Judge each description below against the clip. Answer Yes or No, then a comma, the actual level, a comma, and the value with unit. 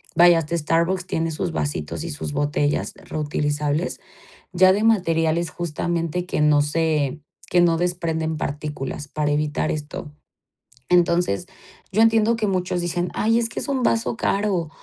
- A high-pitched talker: No, medium, 165 Hz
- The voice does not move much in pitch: No, average, 3.2 semitones